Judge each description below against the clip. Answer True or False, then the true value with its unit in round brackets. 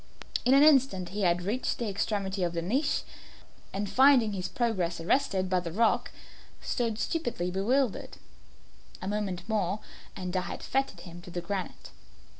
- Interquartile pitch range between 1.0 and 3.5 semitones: False (4.8 semitones)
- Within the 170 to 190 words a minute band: False (160 wpm)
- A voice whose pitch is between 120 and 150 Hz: False (200 Hz)